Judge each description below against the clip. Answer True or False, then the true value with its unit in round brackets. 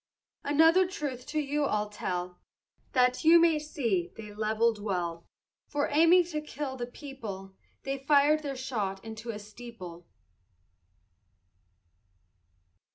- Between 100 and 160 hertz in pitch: False (250 Hz)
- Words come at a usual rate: False (125 wpm)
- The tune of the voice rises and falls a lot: True (6.2 semitones)